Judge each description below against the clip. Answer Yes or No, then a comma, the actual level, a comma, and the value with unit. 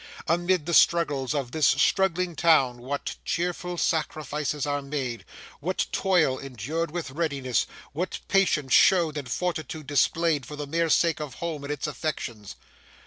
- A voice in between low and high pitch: Yes, medium, 150 Hz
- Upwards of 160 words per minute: No, average, 145 wpm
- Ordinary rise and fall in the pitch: Yes, average, 3.5 semitones